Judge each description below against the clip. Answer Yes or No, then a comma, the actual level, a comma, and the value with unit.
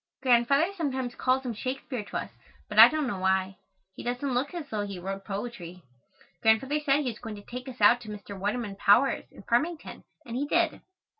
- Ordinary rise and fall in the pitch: Yes, average, 4.9 semitones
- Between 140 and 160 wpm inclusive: No, fast, 205 wpm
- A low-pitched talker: No, high, 245 Hz